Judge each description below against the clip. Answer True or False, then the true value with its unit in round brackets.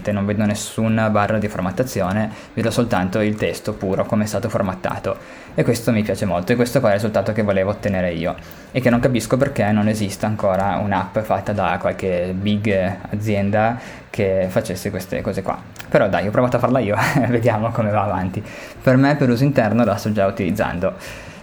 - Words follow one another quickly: True (195 wpm)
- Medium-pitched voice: False (105 Hz)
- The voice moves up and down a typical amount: True (3.2 semitones)